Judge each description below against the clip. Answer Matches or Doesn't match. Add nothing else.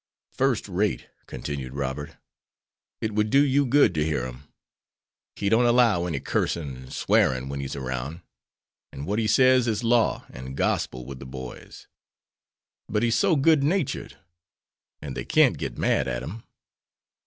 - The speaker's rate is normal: Matches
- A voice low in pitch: Matches